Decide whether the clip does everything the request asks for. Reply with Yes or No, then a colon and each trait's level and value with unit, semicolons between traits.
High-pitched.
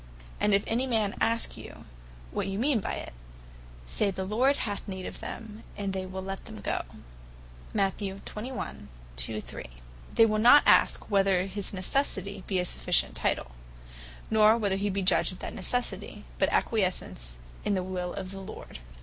Yes: high, 195 Hz